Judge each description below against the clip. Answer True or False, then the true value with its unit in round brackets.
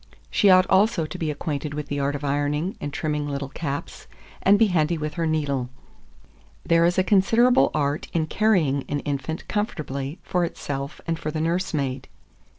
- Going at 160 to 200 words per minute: True (180 wpm)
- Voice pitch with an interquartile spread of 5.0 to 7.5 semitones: False (3.7 semitones)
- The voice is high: False (155 Hz)